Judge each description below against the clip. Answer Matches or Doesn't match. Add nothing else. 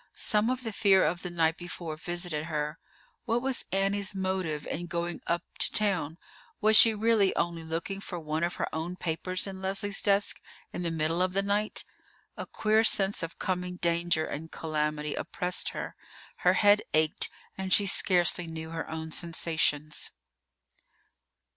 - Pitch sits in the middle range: Matches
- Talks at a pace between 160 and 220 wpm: Matches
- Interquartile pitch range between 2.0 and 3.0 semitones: Doesn't match